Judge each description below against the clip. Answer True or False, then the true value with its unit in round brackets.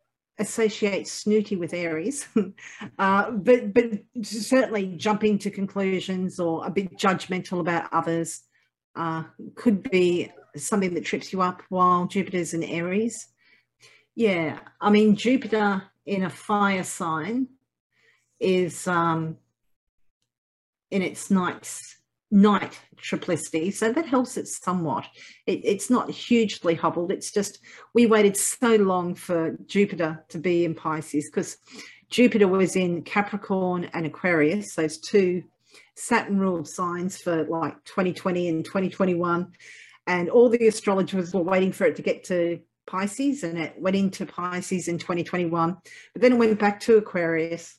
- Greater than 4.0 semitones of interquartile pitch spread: False (3.5 semitones)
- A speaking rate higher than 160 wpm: False (135 wpm)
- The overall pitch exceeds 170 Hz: True (185 Hz)